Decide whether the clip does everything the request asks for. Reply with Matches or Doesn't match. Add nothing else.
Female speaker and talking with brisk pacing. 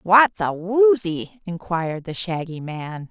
Doesn't match